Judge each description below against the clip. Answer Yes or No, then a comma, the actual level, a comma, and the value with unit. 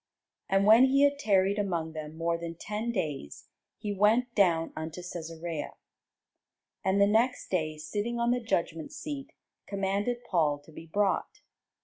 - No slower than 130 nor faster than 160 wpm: Yes, average, 150 wpm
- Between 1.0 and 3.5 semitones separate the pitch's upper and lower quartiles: No, wide, 5.5 semitones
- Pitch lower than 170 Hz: No, high, 195 Hz